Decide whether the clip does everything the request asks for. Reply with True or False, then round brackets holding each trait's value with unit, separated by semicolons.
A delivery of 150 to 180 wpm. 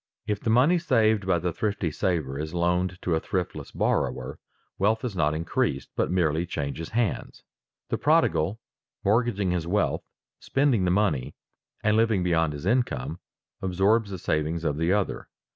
True (160 wpm)